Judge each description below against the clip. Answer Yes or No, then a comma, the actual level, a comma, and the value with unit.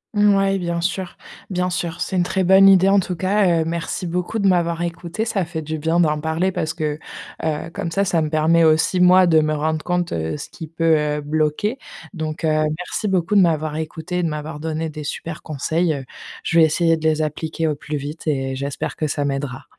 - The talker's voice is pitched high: No, medium, 165 Hz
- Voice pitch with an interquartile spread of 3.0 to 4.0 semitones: No, narrow, 2.6 semitones